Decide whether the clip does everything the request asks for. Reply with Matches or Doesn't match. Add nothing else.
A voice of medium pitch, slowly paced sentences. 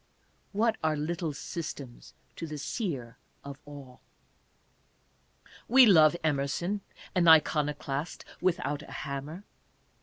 Matches